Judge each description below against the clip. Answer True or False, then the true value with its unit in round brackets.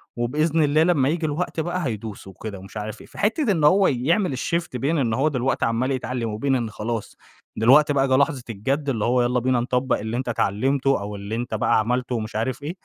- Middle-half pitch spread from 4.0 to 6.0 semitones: True (4.5 semitones)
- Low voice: True (130 Hz)